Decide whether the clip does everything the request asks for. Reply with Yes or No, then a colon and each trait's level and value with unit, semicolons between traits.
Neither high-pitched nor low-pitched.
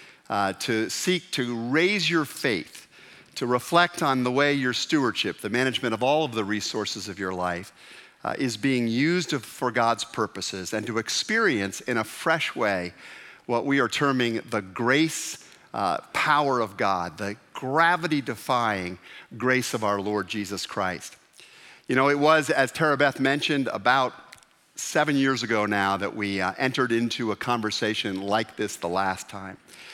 No: low, 120 Hz